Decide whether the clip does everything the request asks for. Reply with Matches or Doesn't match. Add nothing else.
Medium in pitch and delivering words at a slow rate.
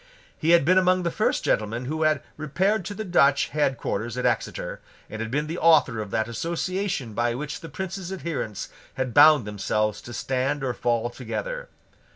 Doesn't match